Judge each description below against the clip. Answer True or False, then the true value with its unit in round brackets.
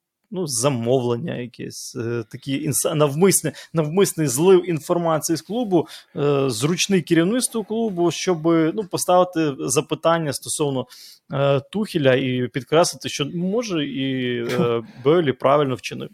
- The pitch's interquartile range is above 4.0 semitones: True (4.5 semitones)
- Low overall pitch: False (155 Hz)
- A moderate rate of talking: True (120 wpm)